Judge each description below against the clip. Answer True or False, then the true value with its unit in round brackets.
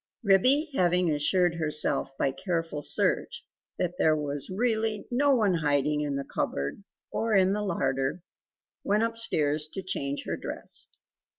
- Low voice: False (175 Hz)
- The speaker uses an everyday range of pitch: False (5.9 semitones)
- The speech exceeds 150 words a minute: False (140 wpm)